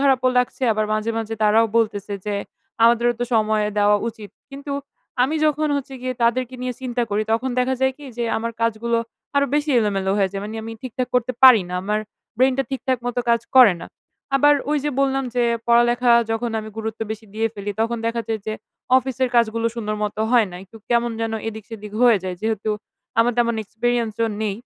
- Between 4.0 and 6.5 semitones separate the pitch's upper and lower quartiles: No, average, 2.7 semitones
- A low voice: No, high, 230 Hz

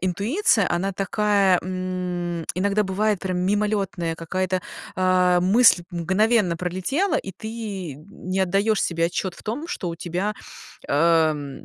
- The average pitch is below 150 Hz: No, medium, 185 Hz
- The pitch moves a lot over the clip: No, average, 2.8 semitones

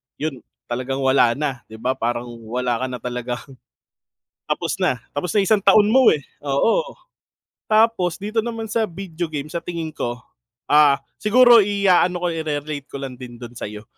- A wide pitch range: Yes, wide, 8.0 semitones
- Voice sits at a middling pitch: Yes, medium, 150 Hz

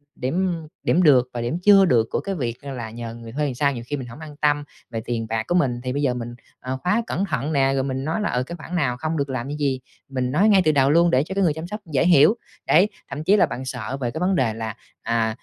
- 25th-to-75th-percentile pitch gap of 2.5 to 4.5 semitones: No, average, 5.0 semitones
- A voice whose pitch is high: No, low, 135 Hz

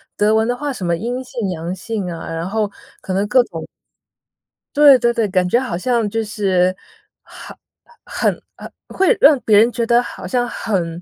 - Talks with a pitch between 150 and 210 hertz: No, high, 220 Hz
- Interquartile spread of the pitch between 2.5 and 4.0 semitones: No, average, 4.8 semitones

